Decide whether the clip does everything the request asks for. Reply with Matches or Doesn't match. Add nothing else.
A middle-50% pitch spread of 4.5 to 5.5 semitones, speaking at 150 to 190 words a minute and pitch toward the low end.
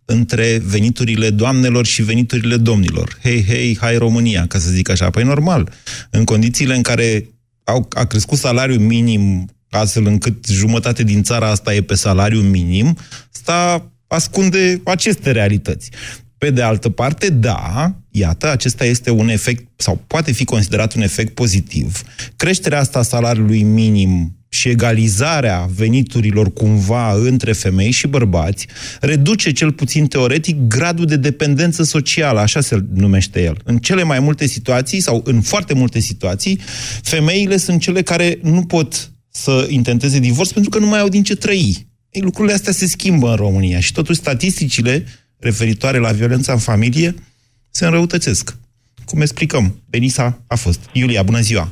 Matches